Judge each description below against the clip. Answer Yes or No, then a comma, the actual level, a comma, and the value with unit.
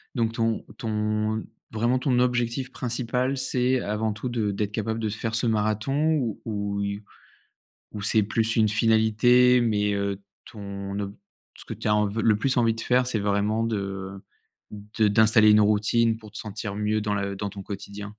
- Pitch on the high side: No, low, 110 Hz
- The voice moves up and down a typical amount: No, narrow, 2.1 semitones